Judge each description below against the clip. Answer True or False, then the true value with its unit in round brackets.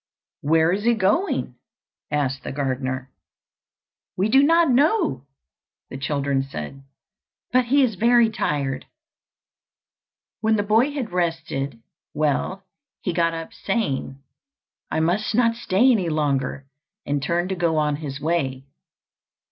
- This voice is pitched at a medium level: True (165 Hz)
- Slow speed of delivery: True (130 wpm)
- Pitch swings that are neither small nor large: False (8.0 semitones)